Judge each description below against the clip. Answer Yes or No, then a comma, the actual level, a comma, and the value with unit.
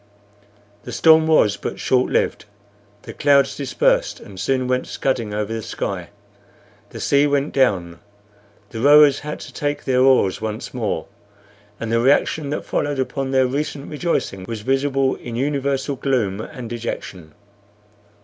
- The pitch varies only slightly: No, average, 4.0 semitones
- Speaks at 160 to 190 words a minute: No, average, 150 wpm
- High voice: No, low, 130 Hz